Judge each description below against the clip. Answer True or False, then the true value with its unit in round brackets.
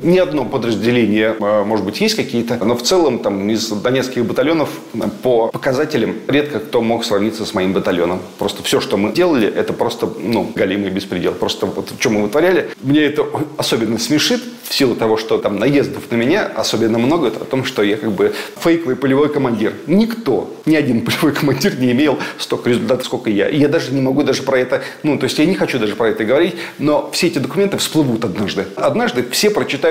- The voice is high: False (130 Hz)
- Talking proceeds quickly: True (205 wpm)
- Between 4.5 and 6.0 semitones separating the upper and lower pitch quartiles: True (5.5 semitones)